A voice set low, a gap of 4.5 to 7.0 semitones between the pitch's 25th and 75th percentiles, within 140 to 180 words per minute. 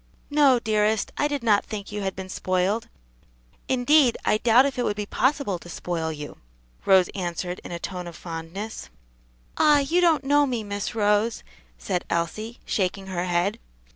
No: high, 205 Hz; average, 5.3 semitones; average, 170 wpm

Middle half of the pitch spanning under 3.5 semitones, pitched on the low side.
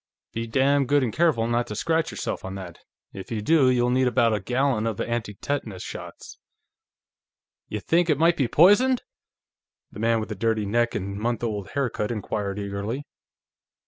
No: average, 4.8 semitones; low, 115 Hz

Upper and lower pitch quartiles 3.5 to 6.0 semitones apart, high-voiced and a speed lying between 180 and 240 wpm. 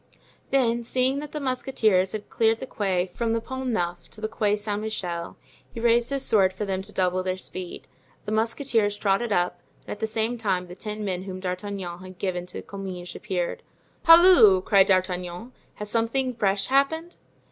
Yes: average, 4.1 semitones; high, 210 Hz; average, 185 wpm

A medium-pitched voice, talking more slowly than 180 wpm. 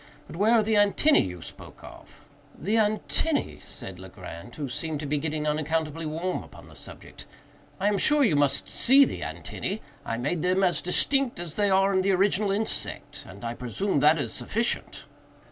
No: medium, 175 Hz; average, 185 wpm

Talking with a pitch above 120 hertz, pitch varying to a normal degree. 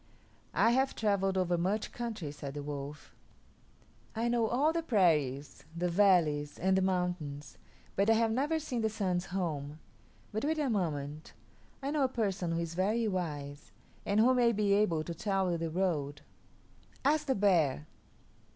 No: high, 190 Hz; wide, 6.1 semitones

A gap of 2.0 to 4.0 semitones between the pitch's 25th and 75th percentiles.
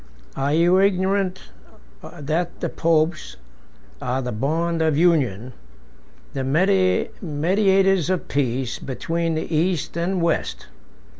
No: average, 4.5 semitones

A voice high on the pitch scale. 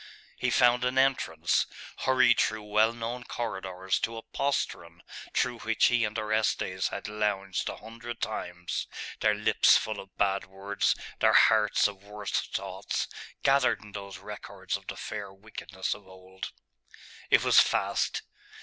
No: low, 105 Hz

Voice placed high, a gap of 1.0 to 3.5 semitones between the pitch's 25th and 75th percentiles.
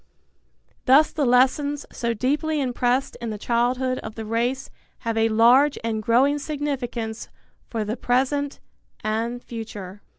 Yes: high, 245 Hz; average, 3.2 semitones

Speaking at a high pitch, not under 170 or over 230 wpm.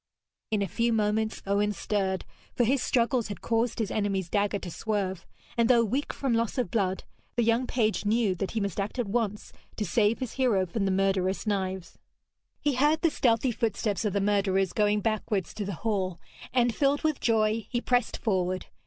Yes: high, 215 Hz; average, 195 wpm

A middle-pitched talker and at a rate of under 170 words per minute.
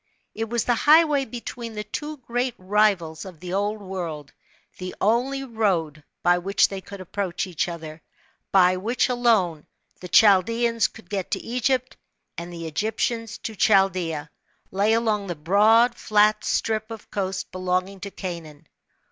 No: high, 200 Hz; average, 155 wpm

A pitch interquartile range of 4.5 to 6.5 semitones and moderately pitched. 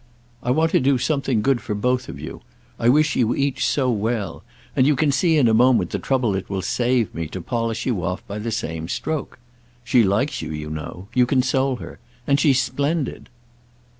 No: average, 4.8 semitones; low, 125 Hz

